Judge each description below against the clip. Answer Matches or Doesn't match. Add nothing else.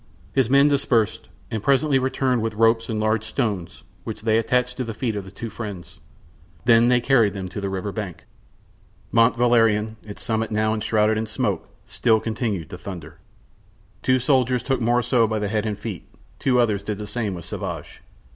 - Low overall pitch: Matches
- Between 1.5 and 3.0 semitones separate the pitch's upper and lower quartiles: Matches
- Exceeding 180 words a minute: Matches